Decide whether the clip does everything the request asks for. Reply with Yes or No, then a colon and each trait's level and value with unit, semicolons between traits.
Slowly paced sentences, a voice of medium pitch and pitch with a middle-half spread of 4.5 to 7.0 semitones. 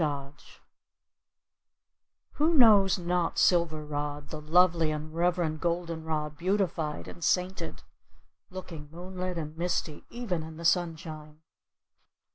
No: slow, 110 wpm; medium, 165 Hz; average, 2.7 semitones